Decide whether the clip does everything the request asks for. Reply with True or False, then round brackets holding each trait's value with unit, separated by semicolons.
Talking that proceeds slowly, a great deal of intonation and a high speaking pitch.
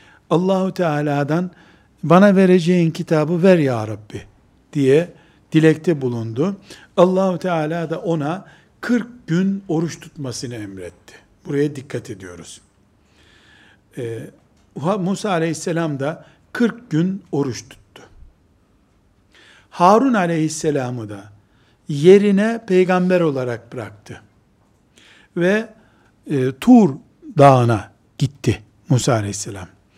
False (90 wpm; 7.3 semitones; 155 Hz)